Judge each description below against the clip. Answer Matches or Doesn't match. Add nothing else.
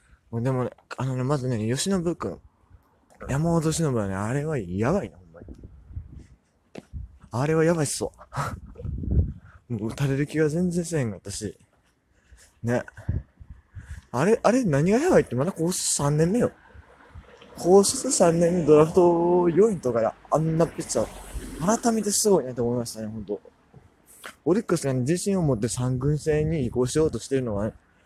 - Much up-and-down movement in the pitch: Matches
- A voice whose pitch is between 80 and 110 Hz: Doesn't match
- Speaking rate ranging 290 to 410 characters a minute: Matches